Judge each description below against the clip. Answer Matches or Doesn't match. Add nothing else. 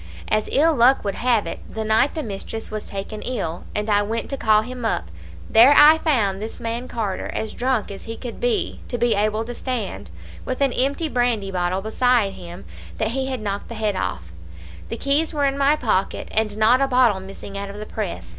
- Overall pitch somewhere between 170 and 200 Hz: Doesn't match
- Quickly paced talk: Matches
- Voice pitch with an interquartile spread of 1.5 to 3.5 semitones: Doesn't match